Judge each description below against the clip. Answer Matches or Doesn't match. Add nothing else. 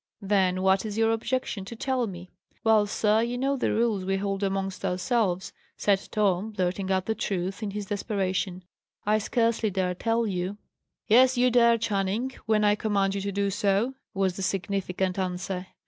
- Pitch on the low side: Doesn't match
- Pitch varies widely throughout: Doesn't match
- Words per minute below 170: Doesn't match